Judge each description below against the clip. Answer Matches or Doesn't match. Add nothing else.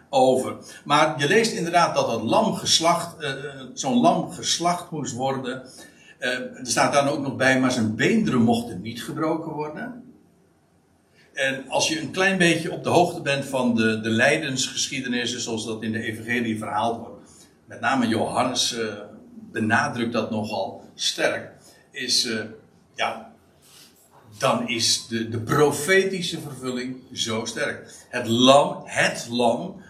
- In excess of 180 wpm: Doesn't match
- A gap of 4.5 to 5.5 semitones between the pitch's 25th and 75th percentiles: Matches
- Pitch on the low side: Matches